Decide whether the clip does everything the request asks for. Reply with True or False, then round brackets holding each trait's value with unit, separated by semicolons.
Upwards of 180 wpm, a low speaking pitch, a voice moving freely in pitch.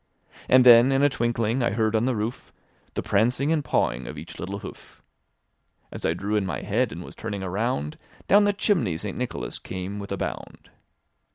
False (195 wpm; 110 Hz; 4.3 semitones)